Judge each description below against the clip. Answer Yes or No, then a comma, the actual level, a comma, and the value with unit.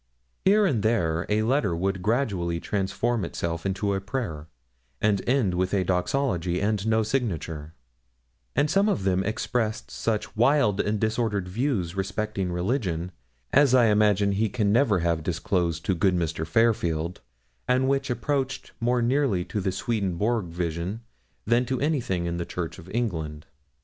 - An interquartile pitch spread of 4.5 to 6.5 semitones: Yes, average, 5.1 semitones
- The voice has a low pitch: Yes, low, 100 Hz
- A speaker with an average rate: Yes, average, 155 wpm